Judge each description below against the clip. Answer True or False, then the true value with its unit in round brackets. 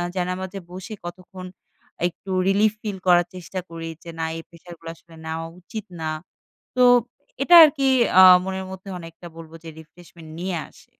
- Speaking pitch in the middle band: True (180 Hz)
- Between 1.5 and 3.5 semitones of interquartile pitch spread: True (2.4 semitones)